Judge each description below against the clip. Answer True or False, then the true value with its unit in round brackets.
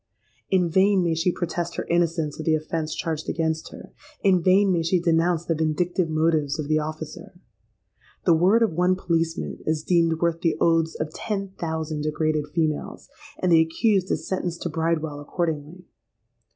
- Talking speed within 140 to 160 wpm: False (170 wpm)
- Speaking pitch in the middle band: True (165 Hz)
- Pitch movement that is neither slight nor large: False (2.0 semitones)